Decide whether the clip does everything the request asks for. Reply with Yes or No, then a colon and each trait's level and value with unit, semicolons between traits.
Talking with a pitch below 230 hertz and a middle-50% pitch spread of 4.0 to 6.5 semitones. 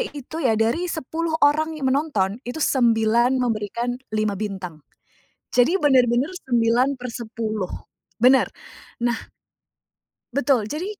No: high, 245 Hz; average, 4.4 semitones